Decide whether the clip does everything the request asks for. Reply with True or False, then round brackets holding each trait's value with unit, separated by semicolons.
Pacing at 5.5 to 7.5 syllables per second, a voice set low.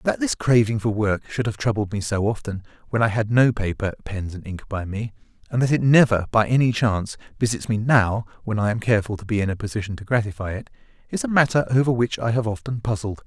True (6.1 syllables/s; 110 Hz)